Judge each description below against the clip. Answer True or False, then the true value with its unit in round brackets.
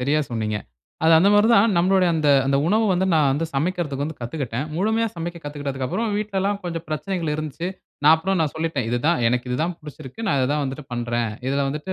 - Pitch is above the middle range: False (155 Hz)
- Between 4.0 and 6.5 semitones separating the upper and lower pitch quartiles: True (5.0 semitones)